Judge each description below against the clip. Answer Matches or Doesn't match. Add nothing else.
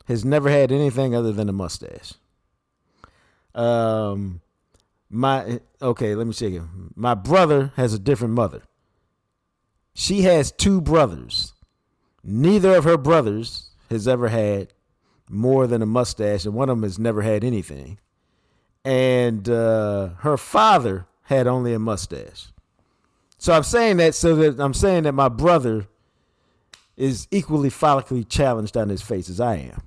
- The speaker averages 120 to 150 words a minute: Matches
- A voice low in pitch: Matches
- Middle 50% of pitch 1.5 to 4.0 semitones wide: Doesn't match